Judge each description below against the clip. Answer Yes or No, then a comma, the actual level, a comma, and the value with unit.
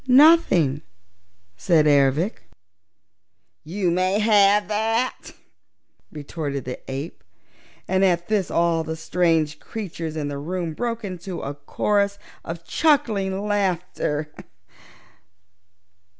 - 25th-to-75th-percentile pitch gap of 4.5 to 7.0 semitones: Yes, average, 4.9 semitones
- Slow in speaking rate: Yes, slow, 100 wpm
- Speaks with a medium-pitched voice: Yes, medium, 175 Hz